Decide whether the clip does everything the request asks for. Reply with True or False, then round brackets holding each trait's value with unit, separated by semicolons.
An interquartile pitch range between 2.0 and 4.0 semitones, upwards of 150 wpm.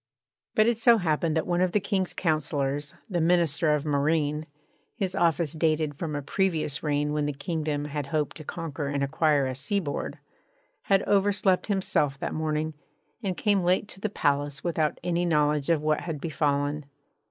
True (3.4 semitones; 175 wpm)